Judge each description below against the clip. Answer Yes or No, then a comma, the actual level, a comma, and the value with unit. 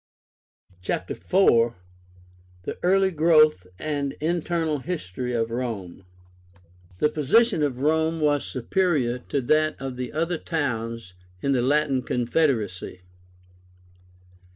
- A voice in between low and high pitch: Yes, medium, 145 Hz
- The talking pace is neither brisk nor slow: No, slow, 105 wpm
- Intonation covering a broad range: No, average, 4.9 semitones